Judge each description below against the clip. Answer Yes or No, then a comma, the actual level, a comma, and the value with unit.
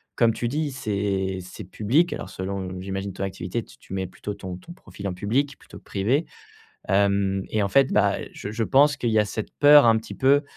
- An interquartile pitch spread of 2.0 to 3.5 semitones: No, average, 5.3 semitones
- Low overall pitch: Yes, low, 105 Hz